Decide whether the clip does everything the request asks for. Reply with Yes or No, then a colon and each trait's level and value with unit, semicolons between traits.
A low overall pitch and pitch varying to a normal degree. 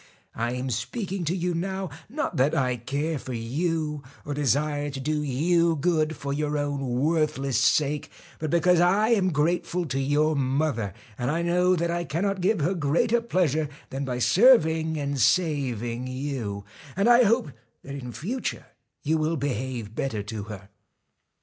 No: medium, 150 Hz; average, 4.7 semitones